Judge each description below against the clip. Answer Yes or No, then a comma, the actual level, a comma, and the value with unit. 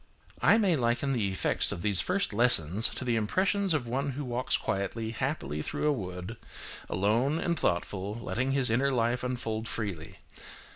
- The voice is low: Yes, low, 120 Hz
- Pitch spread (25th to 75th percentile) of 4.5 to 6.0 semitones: Yes, average, 5.0 semitones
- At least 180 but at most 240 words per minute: No, average, 165 wpm